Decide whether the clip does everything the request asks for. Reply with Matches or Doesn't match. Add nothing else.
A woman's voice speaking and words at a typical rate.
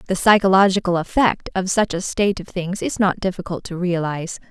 Matches